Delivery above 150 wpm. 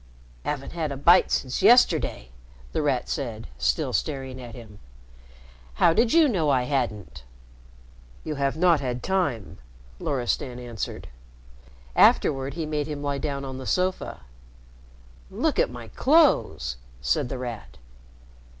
No: slow, 135 wpm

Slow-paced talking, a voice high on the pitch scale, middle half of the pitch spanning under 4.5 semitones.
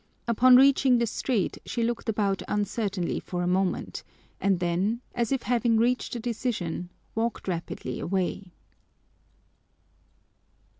Yes: slow, 120 wpm; high, 220 Hz; average, 4.1 semitones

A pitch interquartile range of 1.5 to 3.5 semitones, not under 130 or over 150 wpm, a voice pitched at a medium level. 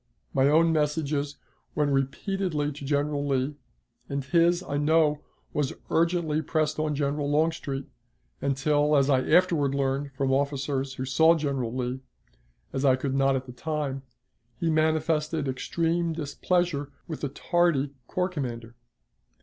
Yes: average, 2.7 semitones; average, 140 wpm; medium, 145 Hz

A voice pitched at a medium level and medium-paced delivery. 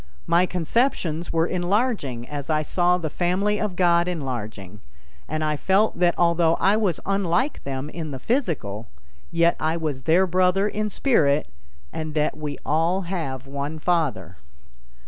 Yes: medium, 170 Hz; average, 150 wpm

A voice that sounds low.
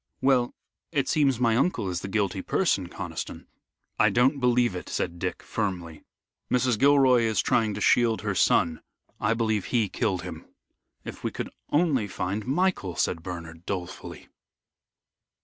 Yes: low, 110 Hz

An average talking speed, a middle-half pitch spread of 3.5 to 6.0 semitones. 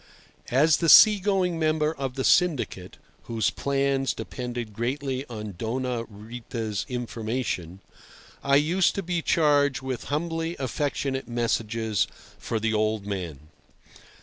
No: slow, 120 wpm; average, 5.1 semitones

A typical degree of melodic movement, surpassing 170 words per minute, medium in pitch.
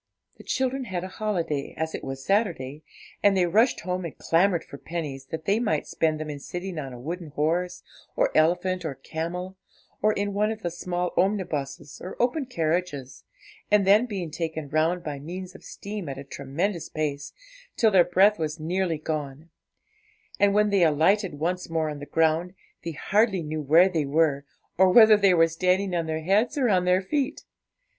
Yes: average, 4.0 semitones; average, 190 wpm; medium, 175 Hz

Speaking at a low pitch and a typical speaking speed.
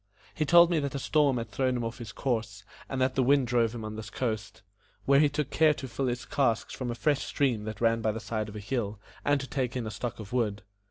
No: low, 120 Hz; fast, 270 wpm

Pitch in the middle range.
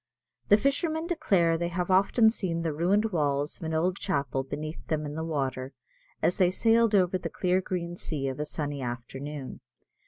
Yes: medium, 170 Hz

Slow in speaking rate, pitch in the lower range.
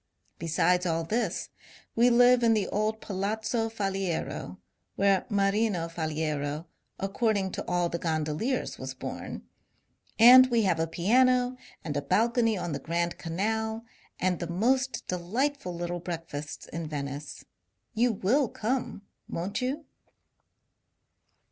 No: slow, 125 wpm; high, 195 Hz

